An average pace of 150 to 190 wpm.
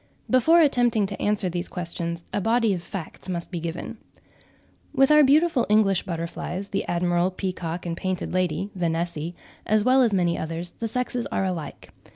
Yes: average, 170 wpm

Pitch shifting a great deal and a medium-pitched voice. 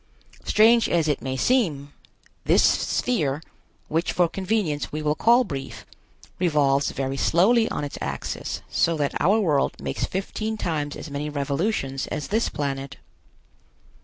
Yes: wide, 6.4 semitones; medium, 150 Hz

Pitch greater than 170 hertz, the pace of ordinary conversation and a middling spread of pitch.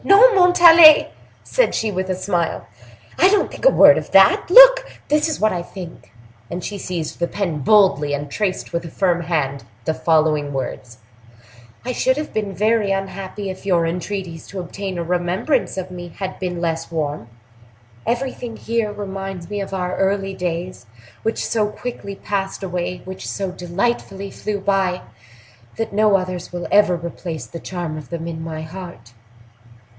Yes: medium, 185 Hz; average, 170 wpm; average, 3.5 semitones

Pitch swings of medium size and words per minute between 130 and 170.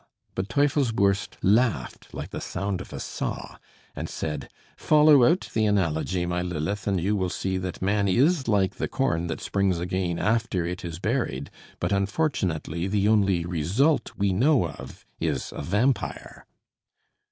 Yes: average, 4.4 semitones; average, 155 wpm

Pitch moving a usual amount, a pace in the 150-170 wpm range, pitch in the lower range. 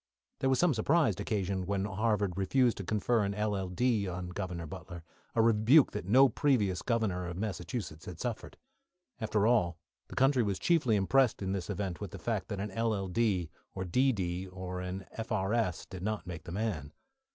No: average, 3.9 semitones; average, 180 wpm; low, 100 Hz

